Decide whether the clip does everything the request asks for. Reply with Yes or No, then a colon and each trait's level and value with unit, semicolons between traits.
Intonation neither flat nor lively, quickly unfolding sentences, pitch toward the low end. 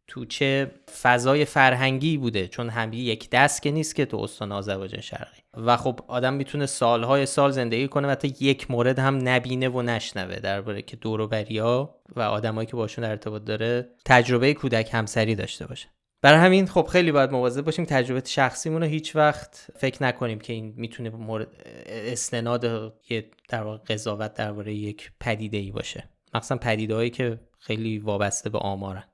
Yes: average, 3.5 semitones; fast, 170 wpm; low, 120 Hz